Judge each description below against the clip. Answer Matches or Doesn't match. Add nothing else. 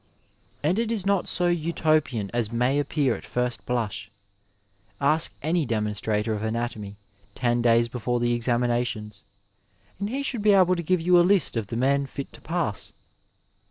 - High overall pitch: Doesn't match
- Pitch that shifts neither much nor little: Doesn't match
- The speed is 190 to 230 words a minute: Doesn't match